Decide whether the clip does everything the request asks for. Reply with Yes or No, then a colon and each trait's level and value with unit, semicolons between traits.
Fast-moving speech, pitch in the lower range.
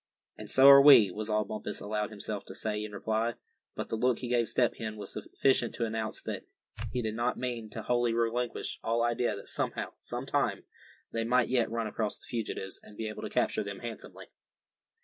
Yes: fast, 210 wpm; low, 115 Hz